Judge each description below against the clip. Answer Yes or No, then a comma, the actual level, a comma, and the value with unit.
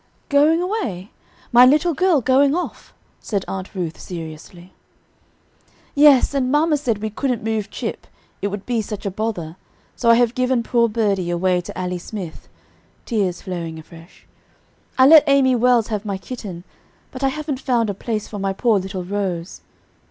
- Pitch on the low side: No, high, 220 Hz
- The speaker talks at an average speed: Yes, average, 165 wpm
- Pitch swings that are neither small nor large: No, wide, 5.7 semitones